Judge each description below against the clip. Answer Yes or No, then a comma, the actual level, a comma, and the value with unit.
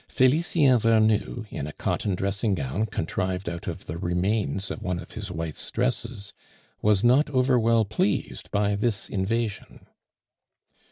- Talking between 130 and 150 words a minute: Yes, average, 145 wpm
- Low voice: Yes, low, 105 Hz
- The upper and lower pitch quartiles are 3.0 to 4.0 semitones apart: Yes, average, 3.7 semitones